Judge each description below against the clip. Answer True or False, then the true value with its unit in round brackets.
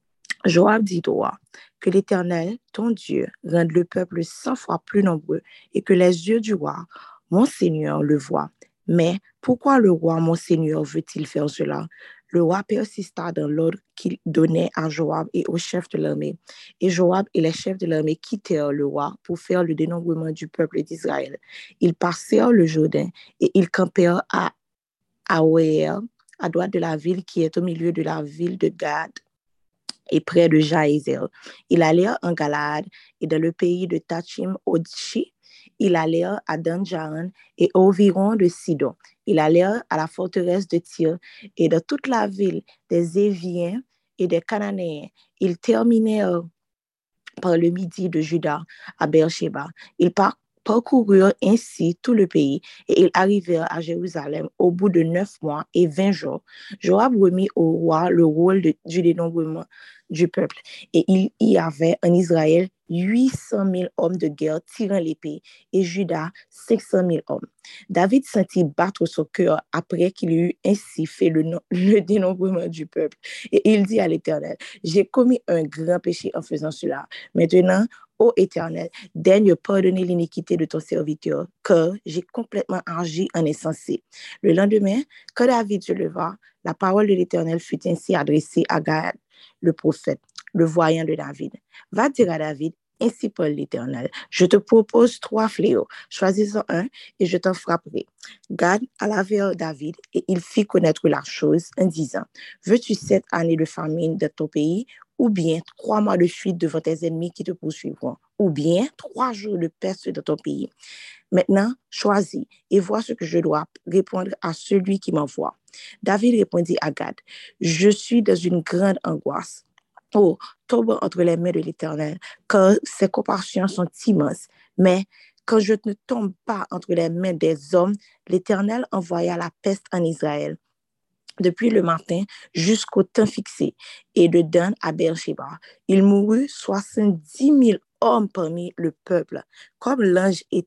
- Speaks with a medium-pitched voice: True (180 Hz)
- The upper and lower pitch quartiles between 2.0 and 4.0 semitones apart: True (3.4 semitones)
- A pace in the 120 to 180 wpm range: True (165 wpm)